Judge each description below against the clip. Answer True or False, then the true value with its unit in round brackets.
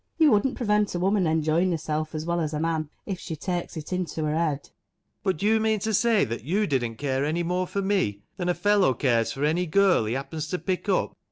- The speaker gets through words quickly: True (245 wpm)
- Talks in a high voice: False (170 Hz)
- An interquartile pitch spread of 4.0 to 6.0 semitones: True (4.5 semitones)